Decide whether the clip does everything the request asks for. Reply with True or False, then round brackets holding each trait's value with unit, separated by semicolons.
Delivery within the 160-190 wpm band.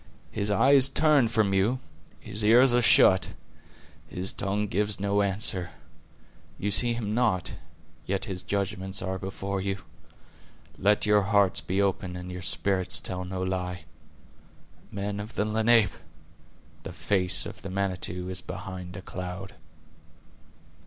False (140 wpm)